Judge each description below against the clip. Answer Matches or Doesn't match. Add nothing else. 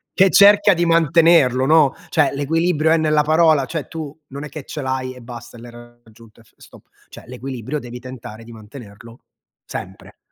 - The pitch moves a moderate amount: Matches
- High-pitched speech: Doesn't match